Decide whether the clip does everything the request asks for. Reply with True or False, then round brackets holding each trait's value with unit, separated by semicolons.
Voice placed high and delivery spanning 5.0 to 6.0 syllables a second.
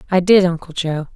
False (175 Hz; 5.7 syllables/s)